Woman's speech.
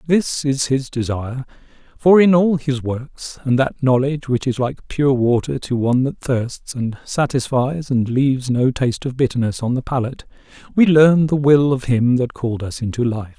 No: male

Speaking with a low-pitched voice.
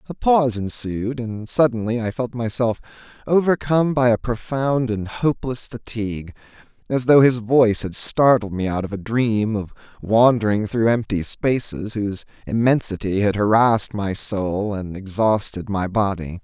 Yes: low, 115 Hz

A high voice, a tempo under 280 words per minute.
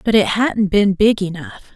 Yes: high, 200 Hz; fast, 205 wpm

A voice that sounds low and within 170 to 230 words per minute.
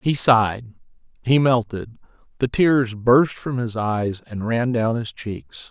No: low, 115 Hz; average, 160 wpm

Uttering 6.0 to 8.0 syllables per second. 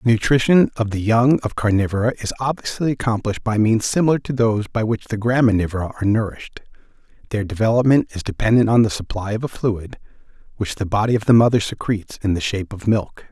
Yes: 6.4 syllables/s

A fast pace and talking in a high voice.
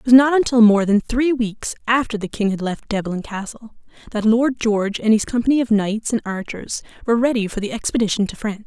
Yes: fast, 220 wpm; high, 225 Hz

